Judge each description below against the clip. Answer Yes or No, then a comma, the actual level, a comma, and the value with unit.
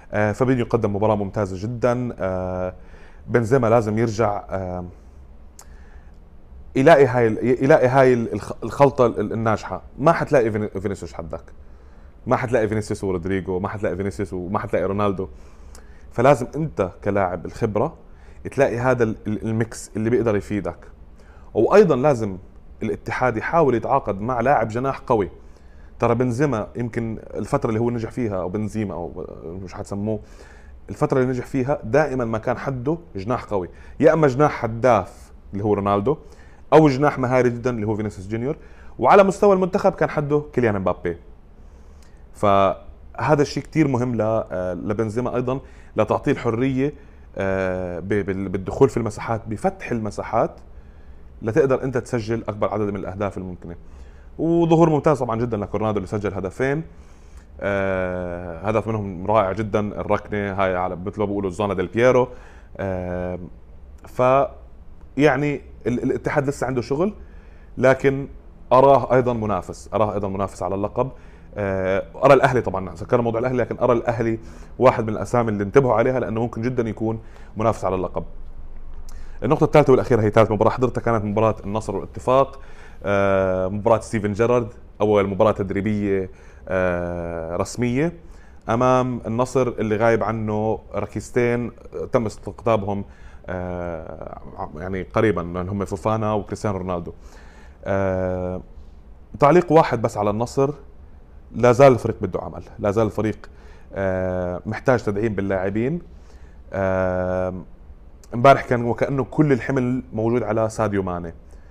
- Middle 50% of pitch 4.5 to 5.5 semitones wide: Yes, average, 5.2 semitones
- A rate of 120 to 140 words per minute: Yes, average, 125 wpm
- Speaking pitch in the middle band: No, low, 105 Hz